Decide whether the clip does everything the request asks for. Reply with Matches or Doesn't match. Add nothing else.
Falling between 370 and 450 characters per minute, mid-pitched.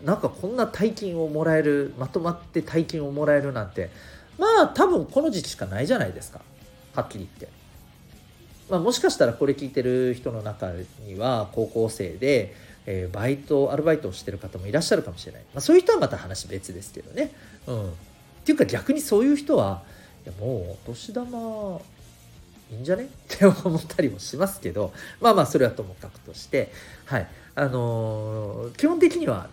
Matches